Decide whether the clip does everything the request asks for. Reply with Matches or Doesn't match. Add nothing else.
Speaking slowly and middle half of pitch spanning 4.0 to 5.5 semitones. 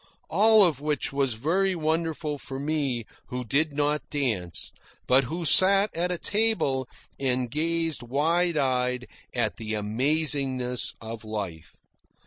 Matches